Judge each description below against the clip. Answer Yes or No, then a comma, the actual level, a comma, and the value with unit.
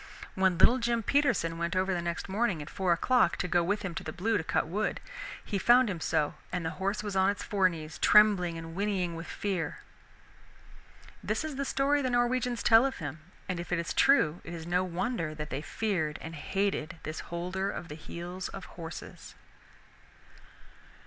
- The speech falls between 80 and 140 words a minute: No, average, 195 wpm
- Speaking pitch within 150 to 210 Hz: Yes, medium, 185 Hz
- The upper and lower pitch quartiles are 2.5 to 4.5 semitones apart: Yes, average, 4.1 semitones